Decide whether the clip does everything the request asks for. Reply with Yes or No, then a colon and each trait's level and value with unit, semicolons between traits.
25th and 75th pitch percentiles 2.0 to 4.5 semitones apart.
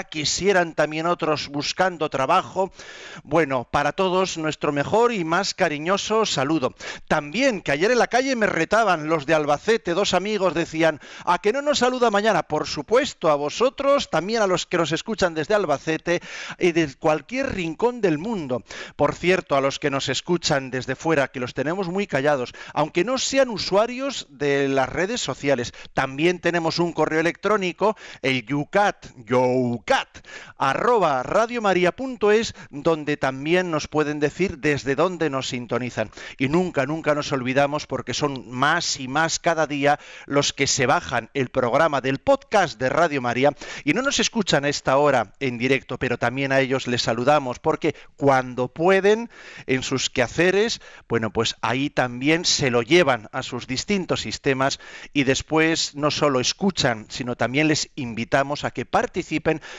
No: average, 5.2 semitones